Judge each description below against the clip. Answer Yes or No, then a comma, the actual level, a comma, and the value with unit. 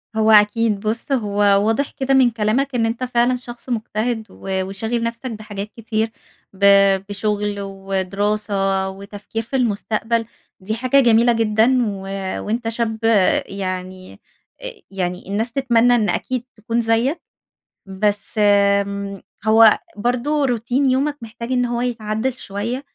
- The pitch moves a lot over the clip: No, average, 3.0 semitones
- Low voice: No, high, 220 Hz